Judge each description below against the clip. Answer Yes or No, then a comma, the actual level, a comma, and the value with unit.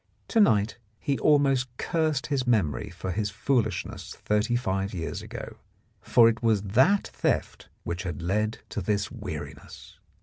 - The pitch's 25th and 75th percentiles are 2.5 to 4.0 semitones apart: No, average, 4.7 semitones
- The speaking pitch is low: Yes, low, 110 Hz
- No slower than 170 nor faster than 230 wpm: No, average, 145 wpm